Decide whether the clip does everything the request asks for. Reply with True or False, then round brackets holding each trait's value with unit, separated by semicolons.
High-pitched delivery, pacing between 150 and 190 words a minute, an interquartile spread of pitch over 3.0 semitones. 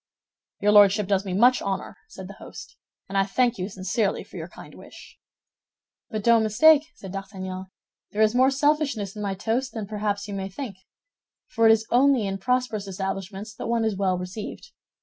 True (210 Hz; 185 wpm; 3.4 semitones)